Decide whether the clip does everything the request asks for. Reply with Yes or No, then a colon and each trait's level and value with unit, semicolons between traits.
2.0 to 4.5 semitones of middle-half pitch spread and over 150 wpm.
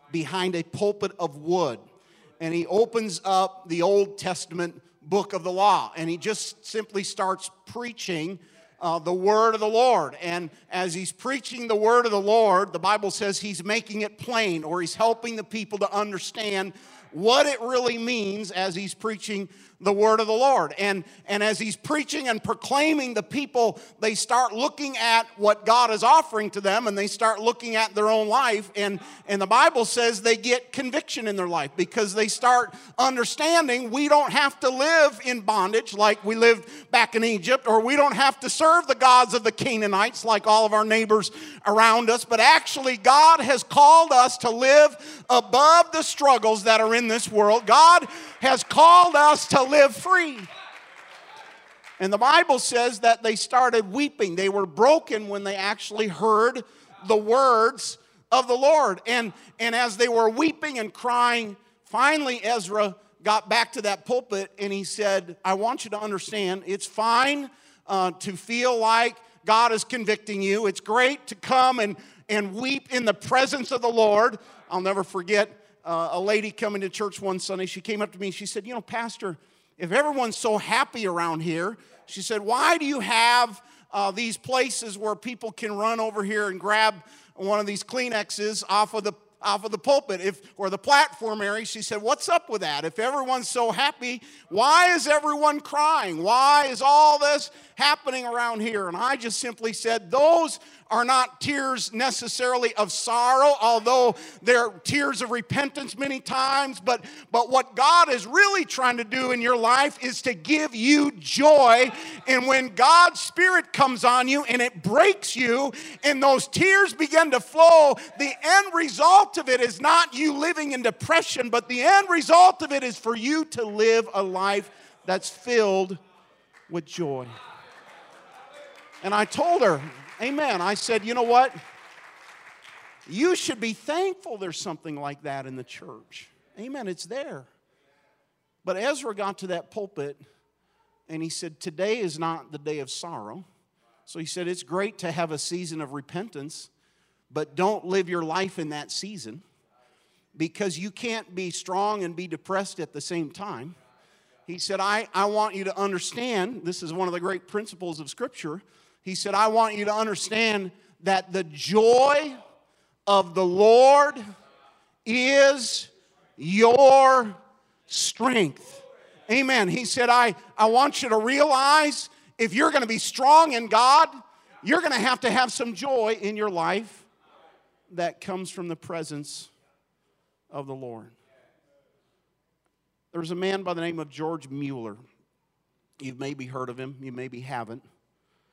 No: average, 5.0 semitones; average, 175 wpm